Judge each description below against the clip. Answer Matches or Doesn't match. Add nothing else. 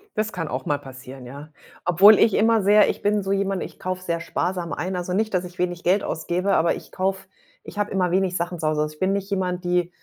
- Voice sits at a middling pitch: Matches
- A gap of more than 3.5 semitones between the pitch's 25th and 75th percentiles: Doesn't match